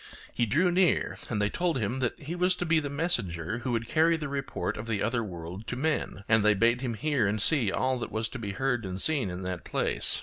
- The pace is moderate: No, fast, 250 wpm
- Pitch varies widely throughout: Yes, wide, 6.2 semitones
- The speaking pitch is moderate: No, low, 120 Hz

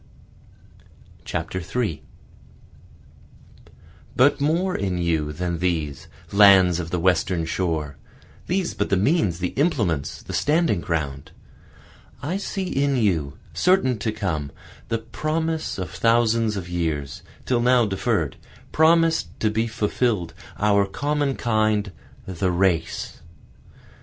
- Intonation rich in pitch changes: Yes, wide, 7.0 semitones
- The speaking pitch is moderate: No, low, 100 Hz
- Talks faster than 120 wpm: No, slow, 115 wpm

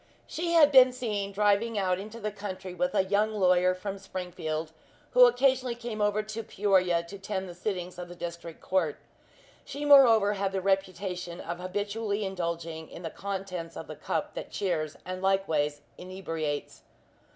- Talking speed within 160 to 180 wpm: Yes, average, 165 wpm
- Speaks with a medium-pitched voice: No, high, 195 Hz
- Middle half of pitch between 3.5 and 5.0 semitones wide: No, average, 3.1 semitones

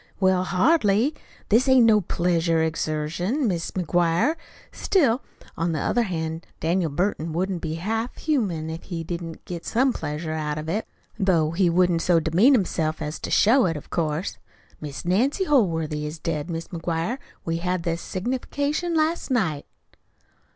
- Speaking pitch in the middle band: Yes, medium, 175 Hz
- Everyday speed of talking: Yes, average, 160 wpm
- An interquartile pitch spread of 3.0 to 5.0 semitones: No, wide, 5.6 semitones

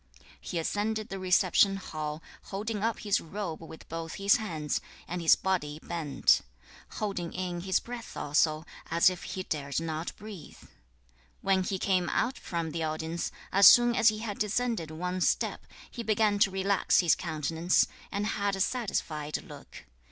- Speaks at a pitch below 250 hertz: Yes, medium, 185 Hz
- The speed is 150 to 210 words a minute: Yes, average, 165 wpm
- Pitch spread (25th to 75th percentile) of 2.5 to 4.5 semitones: Yes, average, 4.1 semitones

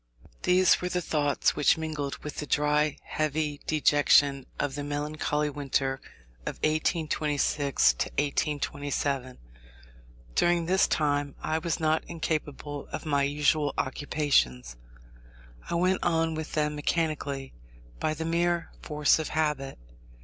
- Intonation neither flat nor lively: No, narrow, 1.7 semitones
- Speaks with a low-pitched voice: No, medium, 150 Hz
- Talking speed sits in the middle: No, slow, 120 wpm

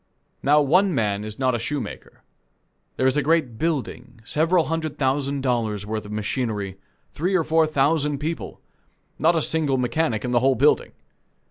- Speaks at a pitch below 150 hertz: Yes, low, 135 Hz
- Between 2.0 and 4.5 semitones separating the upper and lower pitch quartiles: No, average, 4.9 semitones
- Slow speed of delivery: No, average, 165 wpm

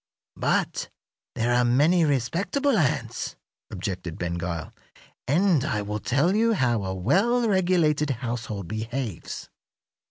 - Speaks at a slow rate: Yes, slow, 120 wpm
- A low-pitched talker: Yes, low, 125 Hz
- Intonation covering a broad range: Yes, wide, 8.7 semitones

